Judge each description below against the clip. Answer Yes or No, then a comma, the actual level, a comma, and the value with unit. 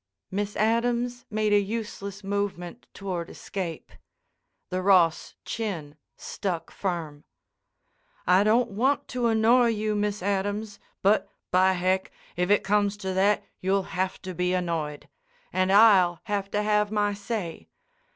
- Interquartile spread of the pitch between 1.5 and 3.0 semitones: Yes, narrow, 2.5 semitones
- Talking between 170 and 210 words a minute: No, slow, 135 wpm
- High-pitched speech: Yes, high, 200 Hz